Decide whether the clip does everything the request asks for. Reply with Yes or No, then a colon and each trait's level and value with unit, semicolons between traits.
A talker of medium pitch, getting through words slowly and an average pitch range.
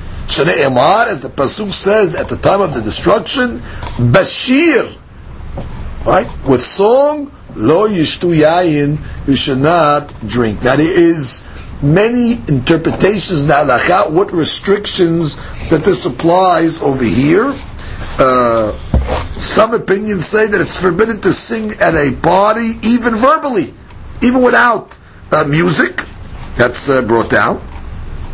No: medium, 170 Hz; slow, 115 wpm; wide, 8.1 semitones